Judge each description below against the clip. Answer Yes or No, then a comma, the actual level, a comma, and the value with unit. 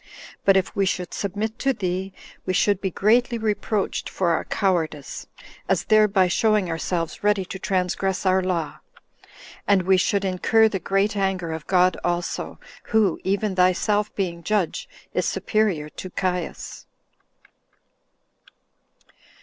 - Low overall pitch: No, high, 190 Hz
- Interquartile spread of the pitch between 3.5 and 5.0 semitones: No, narrow, 2.5 semitones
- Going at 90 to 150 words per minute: Yes, slow, 135 wpm